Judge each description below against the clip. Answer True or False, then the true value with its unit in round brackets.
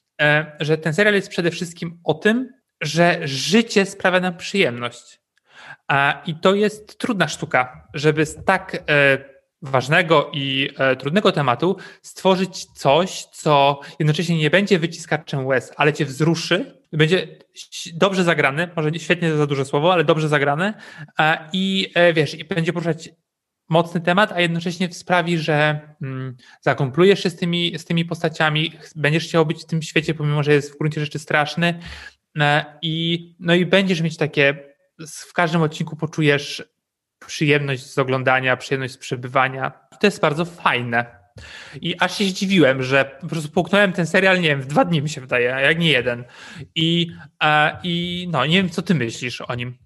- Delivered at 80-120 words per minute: False (160 wpm)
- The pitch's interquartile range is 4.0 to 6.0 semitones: False (3.5 semitones)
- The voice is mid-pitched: True (160 Hz)